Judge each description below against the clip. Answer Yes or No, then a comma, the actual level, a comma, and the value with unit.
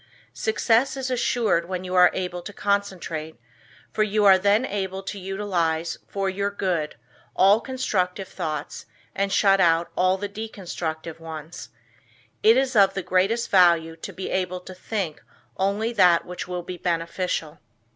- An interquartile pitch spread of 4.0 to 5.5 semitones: No, average, 2.8 semitones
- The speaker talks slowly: No, average, 155 wpm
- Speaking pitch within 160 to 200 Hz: Yes, high, 190 Hz